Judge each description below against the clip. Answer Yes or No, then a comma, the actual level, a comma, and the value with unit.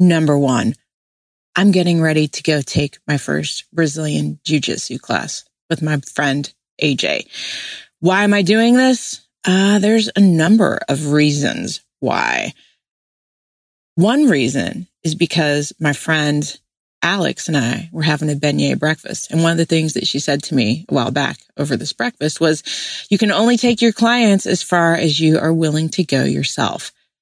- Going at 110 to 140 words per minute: No, average, 170 wpm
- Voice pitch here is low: No, medium, 160 Hz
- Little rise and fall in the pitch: No, average, 4.5 semitones